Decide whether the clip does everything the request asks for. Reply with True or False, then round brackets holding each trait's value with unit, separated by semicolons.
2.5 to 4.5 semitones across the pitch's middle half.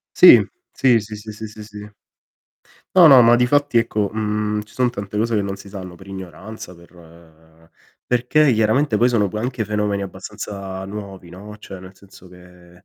True (2.8 semitones)